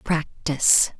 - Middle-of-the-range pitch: Yes, medium, 150 Hz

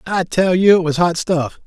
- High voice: No, medium, 175 Hz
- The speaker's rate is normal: No, fast, 250 wpm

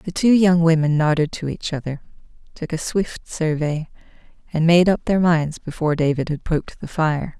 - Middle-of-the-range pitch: Yes, medium, 160 Hz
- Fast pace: No, average, 185 wpm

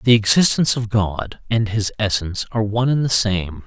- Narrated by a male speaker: Yes, male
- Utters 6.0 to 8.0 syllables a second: No, 5.5 syllables/s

